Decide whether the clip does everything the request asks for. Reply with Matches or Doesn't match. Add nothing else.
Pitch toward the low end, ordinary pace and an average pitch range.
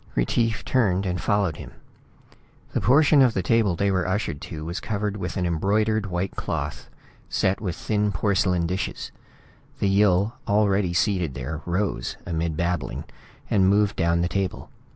Matches